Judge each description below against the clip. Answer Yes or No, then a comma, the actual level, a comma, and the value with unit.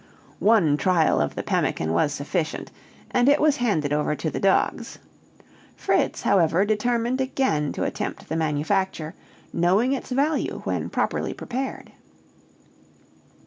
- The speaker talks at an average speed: No, slow, 130 wpm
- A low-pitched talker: No, high, 190 Hz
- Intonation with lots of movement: Yes, wide, 8.1 semitones